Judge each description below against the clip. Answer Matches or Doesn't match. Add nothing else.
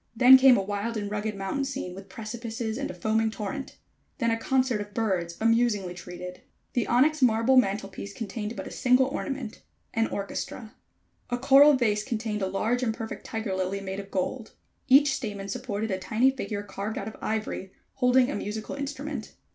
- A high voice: Matches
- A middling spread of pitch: Matches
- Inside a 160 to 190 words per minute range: Matches